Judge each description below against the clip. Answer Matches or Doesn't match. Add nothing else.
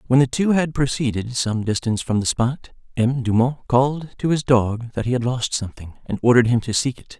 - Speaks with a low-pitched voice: Matches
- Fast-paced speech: Matches